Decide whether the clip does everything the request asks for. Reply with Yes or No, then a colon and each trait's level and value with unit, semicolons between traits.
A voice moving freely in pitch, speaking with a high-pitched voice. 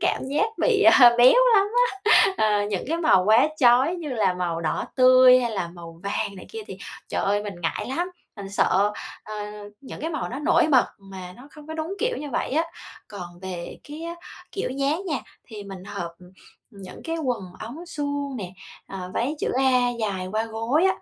Yes: wide, 7.4 semitones; high, 245 Hz